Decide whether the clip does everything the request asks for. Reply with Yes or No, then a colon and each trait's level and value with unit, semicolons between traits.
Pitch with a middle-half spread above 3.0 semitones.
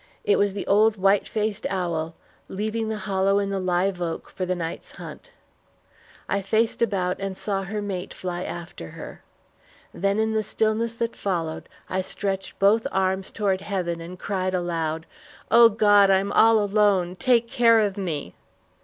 No: narrow, 2.6 semitones